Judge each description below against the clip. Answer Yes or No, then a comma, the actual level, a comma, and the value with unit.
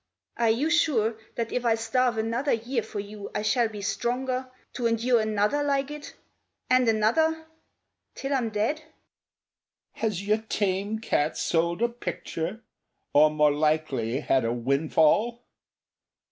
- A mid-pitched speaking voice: No, high, 220 Hz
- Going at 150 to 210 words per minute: No, average, 140 wpm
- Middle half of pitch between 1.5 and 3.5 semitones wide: No, average, 4.9 semitones